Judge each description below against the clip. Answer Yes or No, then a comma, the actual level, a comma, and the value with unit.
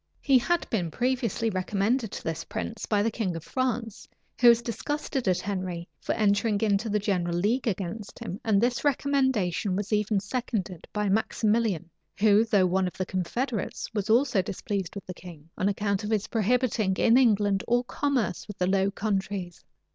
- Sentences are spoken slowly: No, average, 180 wpm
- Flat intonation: No, average, 3.7 semitones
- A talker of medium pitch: No, high, 205 Hz